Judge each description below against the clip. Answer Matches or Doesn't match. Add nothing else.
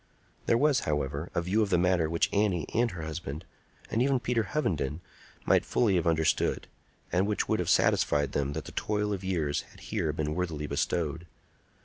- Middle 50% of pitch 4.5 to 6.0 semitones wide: Matches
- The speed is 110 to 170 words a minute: Doesn't match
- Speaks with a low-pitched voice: Matches